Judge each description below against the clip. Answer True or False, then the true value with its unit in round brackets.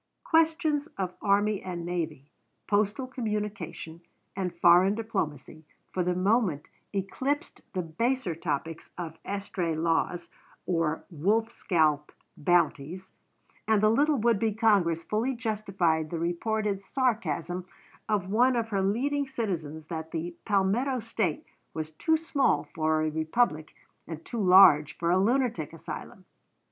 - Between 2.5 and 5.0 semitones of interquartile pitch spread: False (5.4 semitones)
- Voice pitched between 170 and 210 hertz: True (190 Hz)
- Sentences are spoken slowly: True (130 wpm)